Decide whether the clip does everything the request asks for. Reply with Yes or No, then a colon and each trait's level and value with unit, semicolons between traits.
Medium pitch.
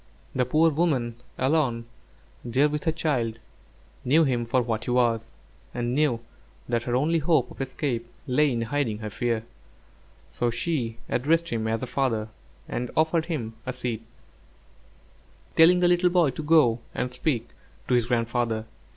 No: low, 125 Hz